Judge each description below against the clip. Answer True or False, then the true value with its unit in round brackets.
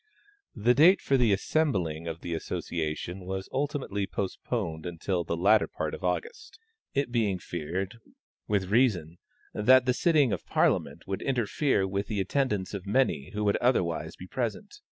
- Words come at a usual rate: True (155 wpm)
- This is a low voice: True (100 Hz)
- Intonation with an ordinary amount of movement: False (6.2 semitones)